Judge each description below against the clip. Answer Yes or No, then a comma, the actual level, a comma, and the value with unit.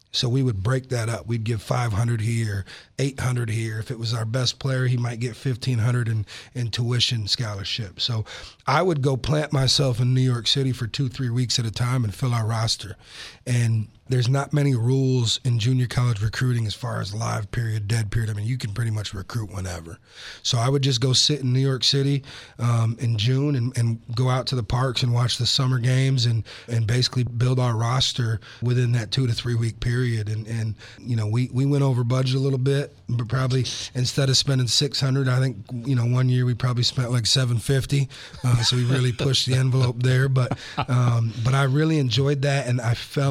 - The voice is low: Yes, low, 125 Hz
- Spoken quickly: Yes, fast, 215 wpm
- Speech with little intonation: Yes, narrow, 2.2 semitones